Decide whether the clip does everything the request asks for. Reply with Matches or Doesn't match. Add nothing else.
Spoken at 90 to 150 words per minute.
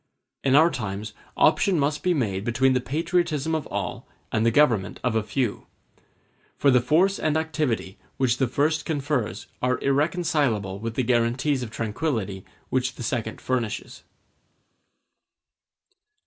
Matches